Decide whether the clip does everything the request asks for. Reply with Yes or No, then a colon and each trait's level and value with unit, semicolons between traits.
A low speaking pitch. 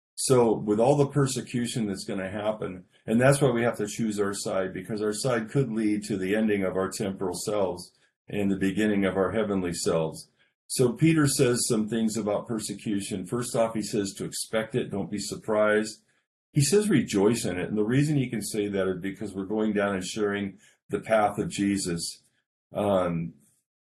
Yes: low, 105 Hz